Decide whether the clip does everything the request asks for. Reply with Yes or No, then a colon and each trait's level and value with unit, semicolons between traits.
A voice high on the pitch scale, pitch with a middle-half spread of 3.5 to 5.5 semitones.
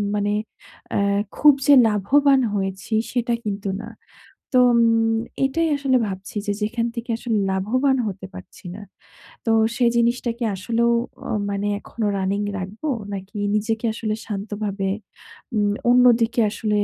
No: high, 215 Hz; average, 3.0 semitones